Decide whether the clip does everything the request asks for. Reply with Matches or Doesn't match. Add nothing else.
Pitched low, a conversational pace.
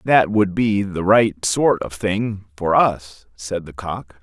Matches